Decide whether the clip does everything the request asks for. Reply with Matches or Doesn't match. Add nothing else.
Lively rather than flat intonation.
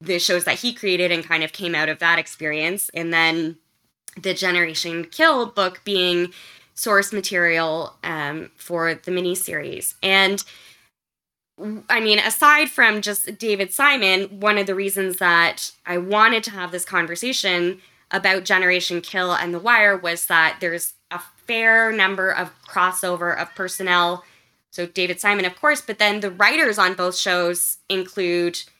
Doesn't match